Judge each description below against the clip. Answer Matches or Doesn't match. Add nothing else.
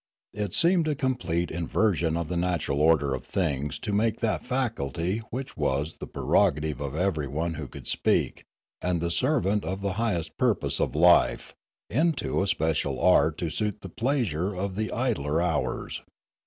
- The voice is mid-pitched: Doesn't match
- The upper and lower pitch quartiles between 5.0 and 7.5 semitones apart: Matches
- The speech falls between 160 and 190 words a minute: Matches